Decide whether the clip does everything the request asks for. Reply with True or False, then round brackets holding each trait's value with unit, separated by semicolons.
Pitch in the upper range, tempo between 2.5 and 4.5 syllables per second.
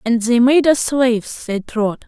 True (240 Hz; 4.1 syllables/s)